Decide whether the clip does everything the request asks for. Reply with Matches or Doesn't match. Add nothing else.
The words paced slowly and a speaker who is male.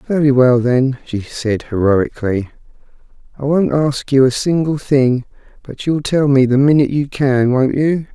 Doesn't match